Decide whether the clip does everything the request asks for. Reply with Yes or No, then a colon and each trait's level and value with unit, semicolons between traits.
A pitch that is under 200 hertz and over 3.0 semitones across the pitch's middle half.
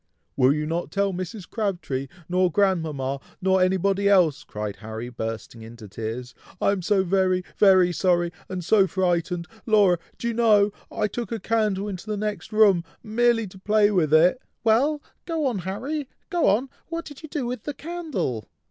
Yes: high, 190 Hz; average, 4.3 semitones